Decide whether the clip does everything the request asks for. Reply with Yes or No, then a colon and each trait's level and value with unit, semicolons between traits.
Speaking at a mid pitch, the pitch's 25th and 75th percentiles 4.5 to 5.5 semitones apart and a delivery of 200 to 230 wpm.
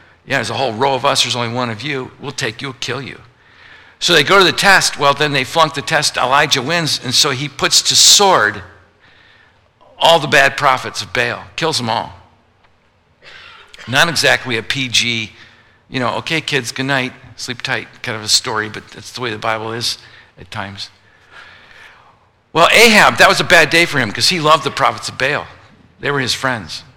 No: low, 130 Hz; average, 4.8 semitones; fast, 205 wpm